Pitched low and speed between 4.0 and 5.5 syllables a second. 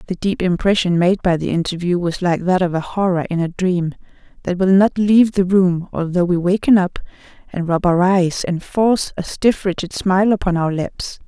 No: medium, 180 Hz; 5.1 syllables/s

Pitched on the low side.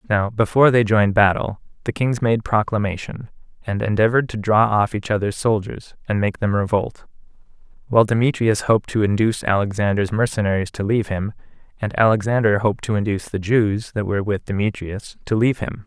Yes: low, 105 Hz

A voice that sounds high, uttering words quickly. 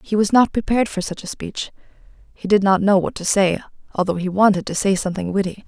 Yes: high, 195 Hz; fast, 235 wpm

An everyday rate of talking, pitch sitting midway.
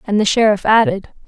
No: average, 190 wpm; high, 210 Hz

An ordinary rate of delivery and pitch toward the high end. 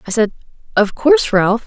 Yes: average, 180 wpm; high, 205 Hz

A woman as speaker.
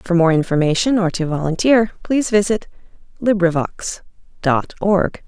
Yes: female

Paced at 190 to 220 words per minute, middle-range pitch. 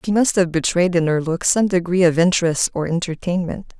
Yes: fast, 205 wpm; medium, 175 Hz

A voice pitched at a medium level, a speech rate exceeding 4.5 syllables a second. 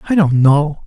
No: medium, 155 Hz; 4.4 syllables/s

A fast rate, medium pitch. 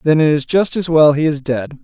Yes: fast, 295 wpm; medium, 150 Hz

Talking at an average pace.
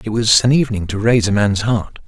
No: fast, 260 wpm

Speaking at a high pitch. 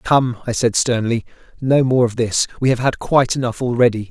No: low, 120 Hz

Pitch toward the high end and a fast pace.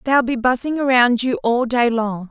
Yes: high, 245 Hz; fast, 210 wpm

